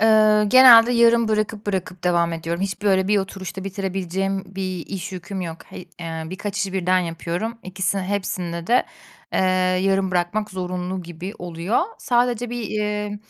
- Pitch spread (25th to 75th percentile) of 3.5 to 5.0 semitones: No, average, 2.8 semitones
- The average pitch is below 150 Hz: No, high, 190 Hz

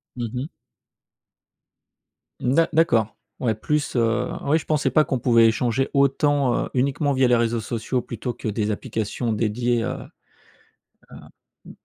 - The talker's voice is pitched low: Yes, low, 125 Hz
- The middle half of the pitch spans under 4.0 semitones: Yes, average, 3.1 semitones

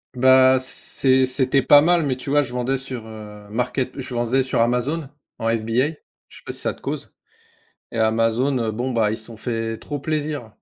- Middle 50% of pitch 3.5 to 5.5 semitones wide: No, average, 2.9 semitones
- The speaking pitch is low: Yes, low, 125 Hz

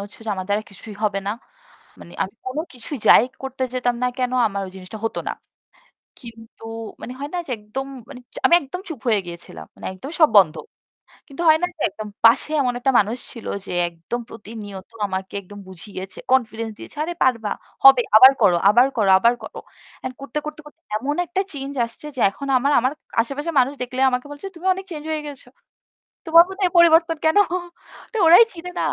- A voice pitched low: No, very high, 250 Hz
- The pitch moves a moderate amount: No, wide, 5.7 semitones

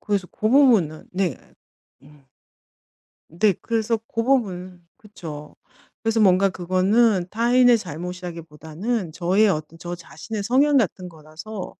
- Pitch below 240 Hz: Yes, medium, 185 Hz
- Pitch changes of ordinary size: Yes, average, 4.9 semitones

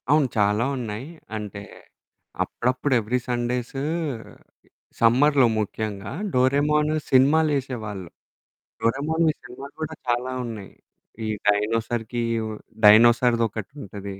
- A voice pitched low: Yes, low, 120 Hz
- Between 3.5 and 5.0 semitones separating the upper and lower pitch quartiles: Yes, average, 4.1 semitones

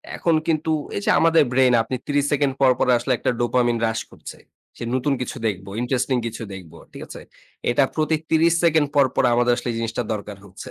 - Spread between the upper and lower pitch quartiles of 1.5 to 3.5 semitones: No, average, 4.1 semitones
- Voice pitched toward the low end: Yes, low, 130 Hz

